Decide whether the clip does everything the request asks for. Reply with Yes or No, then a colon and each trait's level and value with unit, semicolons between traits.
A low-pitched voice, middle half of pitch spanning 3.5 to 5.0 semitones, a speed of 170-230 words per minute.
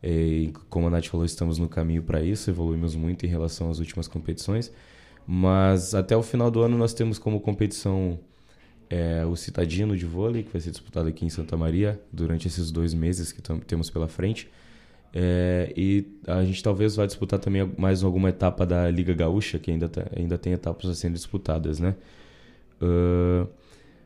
No: very low, 90 Hz; average, 3.0 semitones; fast, 185 wpm